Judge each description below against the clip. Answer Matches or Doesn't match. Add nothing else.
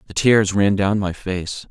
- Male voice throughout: Matches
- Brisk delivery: Matches